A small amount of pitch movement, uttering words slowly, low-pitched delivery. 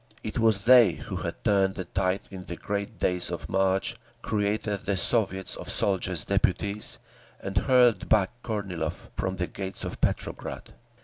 No: narrow, 2.2 semitones; average, 160 wpm; low, 100 Hz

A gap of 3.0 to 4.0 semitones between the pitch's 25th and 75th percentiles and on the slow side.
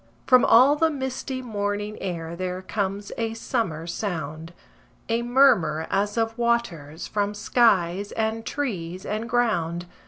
No: average, 5.2 semitones; slow, 130 wpm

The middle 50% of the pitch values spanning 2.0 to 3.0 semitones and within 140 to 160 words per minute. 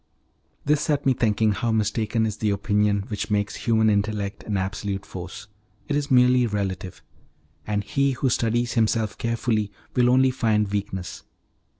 Yes: average, 2.7 semitones; average, 155 wpm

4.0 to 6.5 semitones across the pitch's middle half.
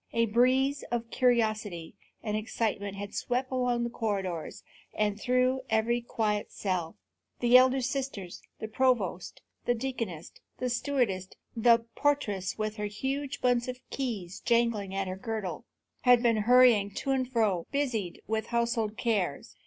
No: average, 3.6 semitones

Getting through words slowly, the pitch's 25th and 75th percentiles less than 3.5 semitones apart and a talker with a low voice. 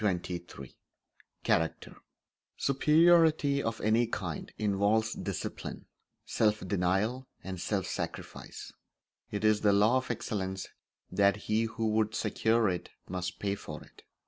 Yes: slow, 125 wpm; average, 3.0 semitones; low, 105 Hz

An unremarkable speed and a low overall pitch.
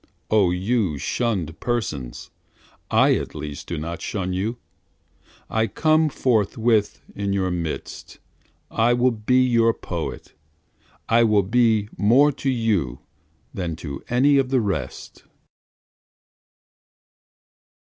No: slow, 115 wpm; low, 110 Hz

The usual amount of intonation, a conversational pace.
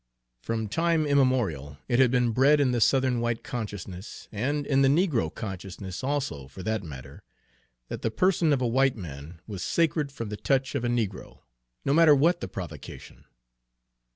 No: wide, 6.4 semitones; average, 175 wpm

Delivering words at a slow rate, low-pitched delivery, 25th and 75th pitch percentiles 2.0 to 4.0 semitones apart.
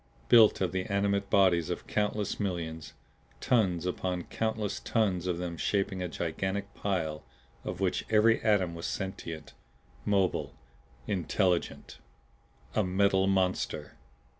Yes: slow, 120 wpm; very low, 95 Hz; narrow, 2.4 semitones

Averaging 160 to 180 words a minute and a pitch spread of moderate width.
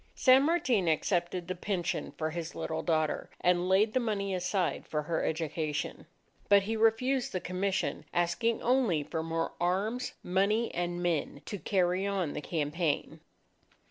No: average, 150 wpm; average, 4.2 semitones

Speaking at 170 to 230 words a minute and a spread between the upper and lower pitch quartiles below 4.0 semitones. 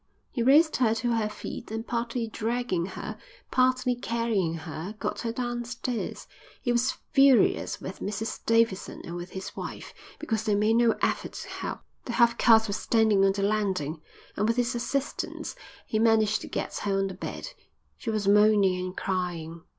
Yes: average, 175 wpm; average, 3.4 semitones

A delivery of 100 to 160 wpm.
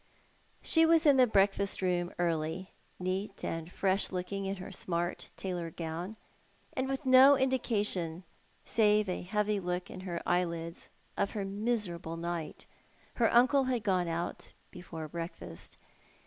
Yes: average, 140 wpm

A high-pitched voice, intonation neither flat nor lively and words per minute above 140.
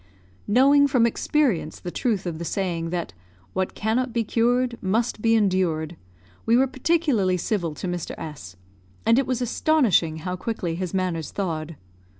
No: high, 195 Hz; wide, 6.0 semitones; average, 160 wpm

